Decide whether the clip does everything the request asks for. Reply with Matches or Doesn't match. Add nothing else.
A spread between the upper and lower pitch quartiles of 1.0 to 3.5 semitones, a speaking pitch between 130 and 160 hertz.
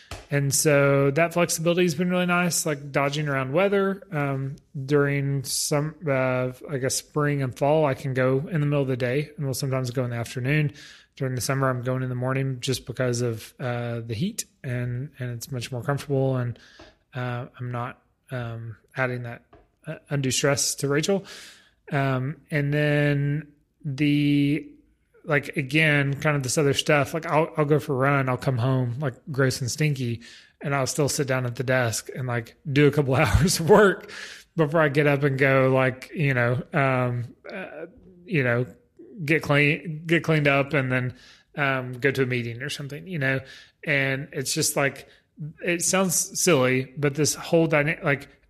Matches